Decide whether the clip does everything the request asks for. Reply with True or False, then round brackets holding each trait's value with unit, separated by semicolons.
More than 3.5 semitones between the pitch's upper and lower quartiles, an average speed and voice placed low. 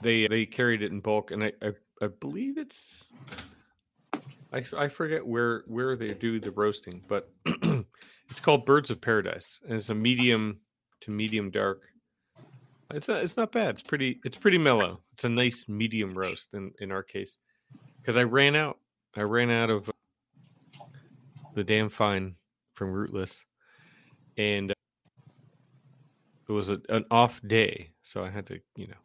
True (4.7 semitones; 165 wpm; 115 Hz)